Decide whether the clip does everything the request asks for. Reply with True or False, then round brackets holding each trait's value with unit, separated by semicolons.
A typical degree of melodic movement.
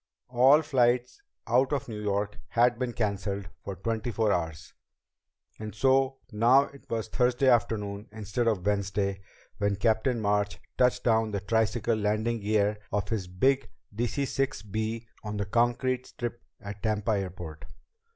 True (3.0 semitones)